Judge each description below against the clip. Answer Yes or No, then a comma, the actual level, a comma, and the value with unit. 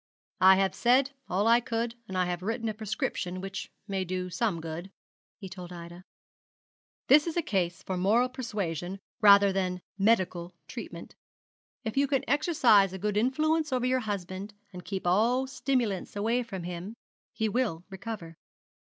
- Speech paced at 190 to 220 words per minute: No, average, 160 wpm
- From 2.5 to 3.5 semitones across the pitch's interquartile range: No, average, 4.6 semitones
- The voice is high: Yes, high, 200 Hz